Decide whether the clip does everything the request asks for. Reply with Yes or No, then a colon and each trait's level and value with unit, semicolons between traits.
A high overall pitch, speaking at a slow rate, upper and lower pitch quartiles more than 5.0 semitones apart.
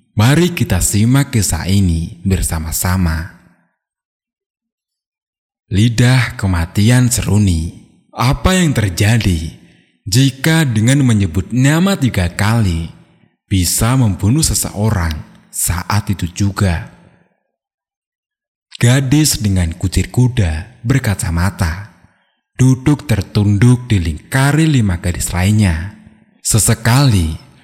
No: low, 105 Hz; slow, 80 wpm; wide, 5.5 semitones